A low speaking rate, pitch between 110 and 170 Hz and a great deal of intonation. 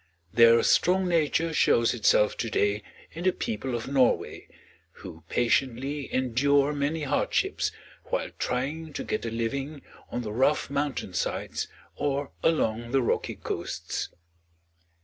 No: slow, 130 wpm; low, 135 Hz; average, 4.1 semitones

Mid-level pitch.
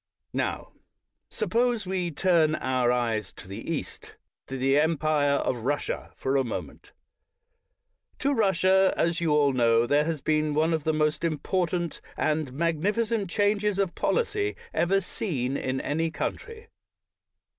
Yes: medium, 160 Hz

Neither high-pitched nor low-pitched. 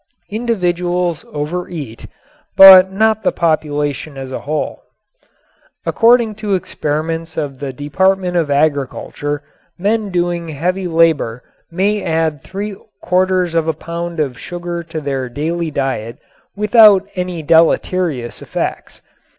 Yes: medium, 170 Hz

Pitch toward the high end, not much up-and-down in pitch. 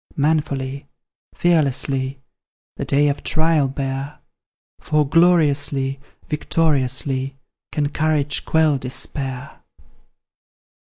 No: medium, 140 Hz; narrow, 2.3 semitones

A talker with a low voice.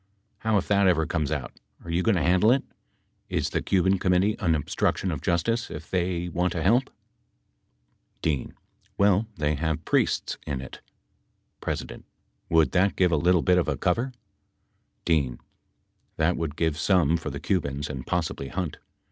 Yes: very low, 85 Hz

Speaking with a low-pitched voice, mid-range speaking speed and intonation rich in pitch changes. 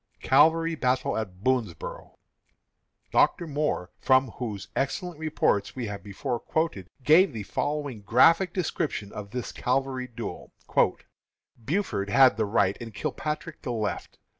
No: low, 130 Hz; slow, 130 wpm; wide, 6.4 semitones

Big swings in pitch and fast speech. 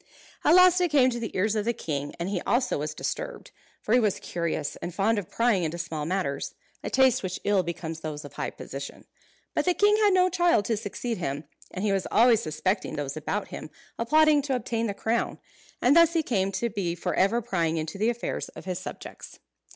Yes: wide, 6.4 semitones; fast, 220 wpm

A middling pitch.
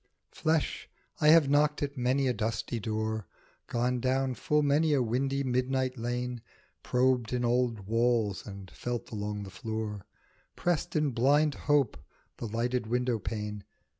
No: low, 125 Hz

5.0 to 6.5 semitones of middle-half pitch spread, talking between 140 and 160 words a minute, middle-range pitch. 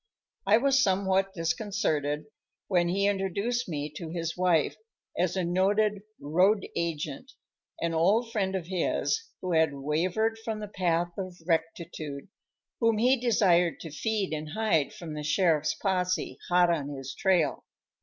No: average, 4.0 semitones; average, 145 wpm; medium, 180 Hz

